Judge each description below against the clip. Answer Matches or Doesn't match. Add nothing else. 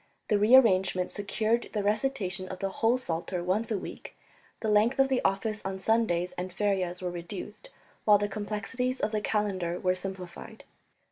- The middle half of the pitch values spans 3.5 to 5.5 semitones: Doesn't match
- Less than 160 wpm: Doesn't match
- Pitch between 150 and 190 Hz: Doesn't match